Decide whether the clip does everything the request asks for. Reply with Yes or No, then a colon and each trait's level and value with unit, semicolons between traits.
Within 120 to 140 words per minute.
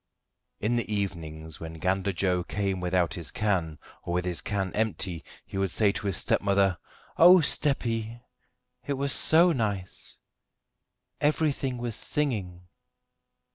Yes: slow, 135 wpm